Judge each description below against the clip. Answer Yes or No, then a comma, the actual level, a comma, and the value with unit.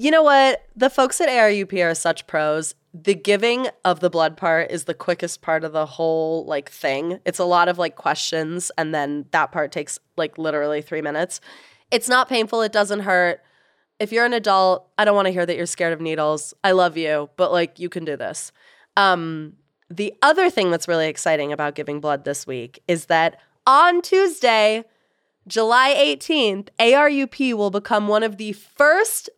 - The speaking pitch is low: No, medium, 180 Hz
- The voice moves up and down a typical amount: No, wide, 5.7 semitones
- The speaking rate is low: No, average, 190 wpm